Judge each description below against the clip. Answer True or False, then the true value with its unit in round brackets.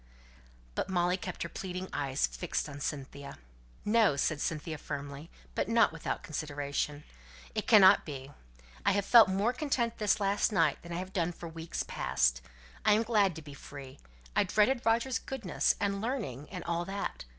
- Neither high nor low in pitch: True (180 Hz)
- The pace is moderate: True (160 wpm)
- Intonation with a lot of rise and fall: True (6.2 semitones)